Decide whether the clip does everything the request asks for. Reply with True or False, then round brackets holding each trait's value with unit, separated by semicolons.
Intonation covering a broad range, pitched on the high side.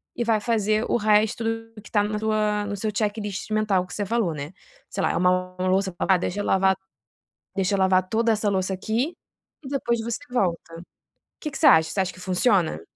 False (2.9 semitones; 205 Hz)